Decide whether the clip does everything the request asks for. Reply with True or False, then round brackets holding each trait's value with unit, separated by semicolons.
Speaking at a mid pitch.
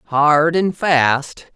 True (150 Hz)